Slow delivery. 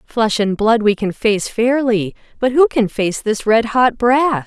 No: average, 200 wpm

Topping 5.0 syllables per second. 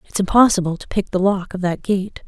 Yes: 5.7 syllables/s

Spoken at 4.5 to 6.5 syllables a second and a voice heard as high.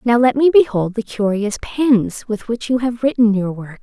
Yes: 4.6 syllables/s; high, 230 Hz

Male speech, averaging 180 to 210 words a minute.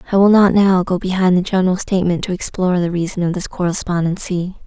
No: female; fast, 205 wpm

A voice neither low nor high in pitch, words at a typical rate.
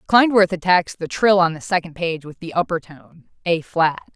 Yes: medium, 170 Hz; average, 190 wpm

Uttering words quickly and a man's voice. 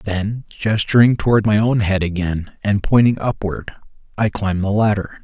No: average, 160 wpm; male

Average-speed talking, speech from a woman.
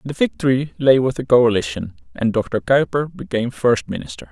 No: average, 165 wpm; male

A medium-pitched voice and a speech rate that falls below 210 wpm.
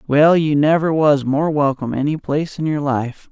Yes: medium, 145 Hz; average, 200 wpm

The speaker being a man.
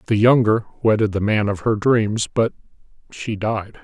Yes: male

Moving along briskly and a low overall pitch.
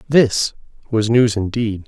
No: slow, 130 wpm; low, 110 Hz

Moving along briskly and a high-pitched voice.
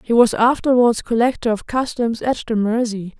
No: average, 170 wpm; high, 230 Hz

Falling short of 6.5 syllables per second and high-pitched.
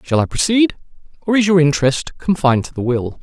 No: 6.0 syllables/s; medium, 160 Hz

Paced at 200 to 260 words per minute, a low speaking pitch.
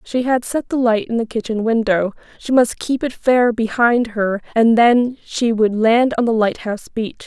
No: fast, 205 wpm; high, 230 Hz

